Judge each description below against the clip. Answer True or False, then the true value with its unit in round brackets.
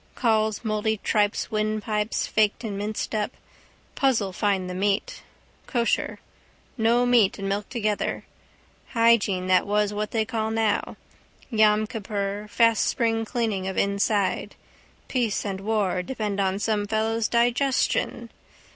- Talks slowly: True (130 wpm)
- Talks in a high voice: True (215 Hz)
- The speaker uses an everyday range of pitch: False (1.9 semitones)